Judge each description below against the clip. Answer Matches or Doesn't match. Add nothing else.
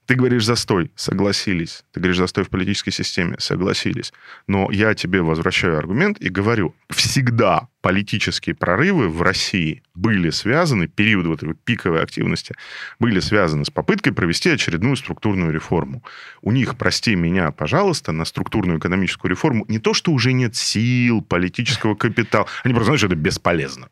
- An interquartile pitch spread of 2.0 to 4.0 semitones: Doesn't match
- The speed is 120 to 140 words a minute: Doesn't match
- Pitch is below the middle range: Matches